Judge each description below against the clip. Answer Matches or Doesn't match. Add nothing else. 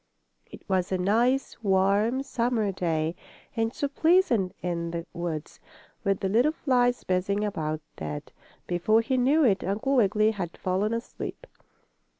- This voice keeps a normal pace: Matches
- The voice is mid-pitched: Doesn't match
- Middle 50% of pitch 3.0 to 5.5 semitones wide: Matches